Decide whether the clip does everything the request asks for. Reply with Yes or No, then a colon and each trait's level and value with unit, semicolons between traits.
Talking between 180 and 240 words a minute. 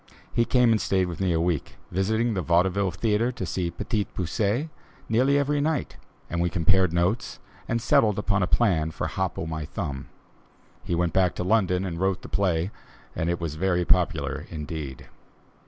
Yes: average, 185 wpm